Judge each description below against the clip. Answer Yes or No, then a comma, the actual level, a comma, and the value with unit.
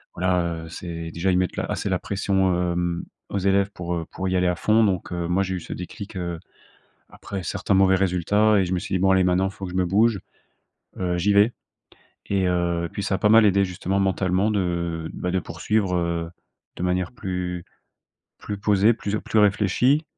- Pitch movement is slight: Yes, narrow, 2.1 semitones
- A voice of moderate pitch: No, very low, 95 Hz